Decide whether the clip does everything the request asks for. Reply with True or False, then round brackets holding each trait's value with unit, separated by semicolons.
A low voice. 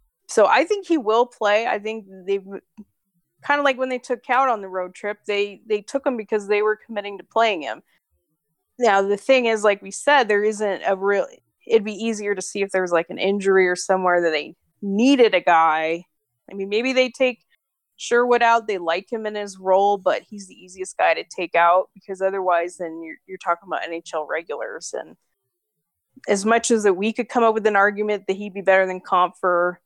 False (200 Hz)